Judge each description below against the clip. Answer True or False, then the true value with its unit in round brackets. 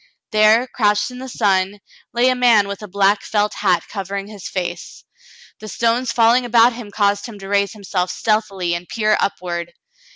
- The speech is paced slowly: False (175 wpm)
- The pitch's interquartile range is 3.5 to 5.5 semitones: False (2.8 semitones)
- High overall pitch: True (210 Hz)